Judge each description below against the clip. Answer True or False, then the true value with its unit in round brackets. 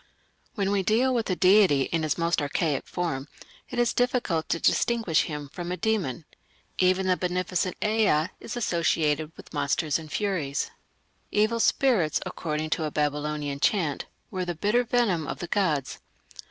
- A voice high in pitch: False (175 Hz)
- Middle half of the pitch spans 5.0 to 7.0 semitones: True (5.3 semitones)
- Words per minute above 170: False (160 wpm)